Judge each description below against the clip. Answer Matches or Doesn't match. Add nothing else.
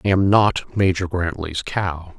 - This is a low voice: Matches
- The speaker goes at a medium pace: Matches